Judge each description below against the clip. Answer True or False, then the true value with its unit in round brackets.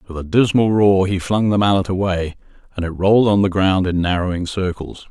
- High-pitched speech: False (95 Hz)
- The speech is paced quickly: True (210 wpm)